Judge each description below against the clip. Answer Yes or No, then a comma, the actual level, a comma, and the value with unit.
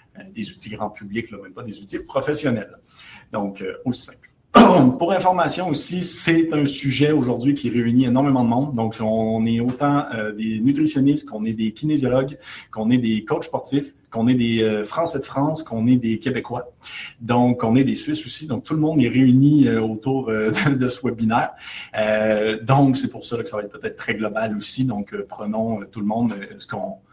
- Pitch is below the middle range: Yes, low, 120 Hz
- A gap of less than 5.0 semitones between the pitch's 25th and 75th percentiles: Yes, average, 4.0 semitones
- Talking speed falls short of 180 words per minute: No, average, 185 wpm